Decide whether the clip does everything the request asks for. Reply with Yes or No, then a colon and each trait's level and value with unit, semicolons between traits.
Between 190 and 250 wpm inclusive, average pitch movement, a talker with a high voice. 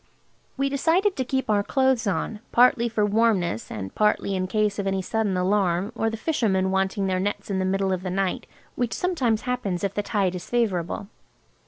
Yes: average, 195 wpm; average, 3.7 semitones; high, 205 Hz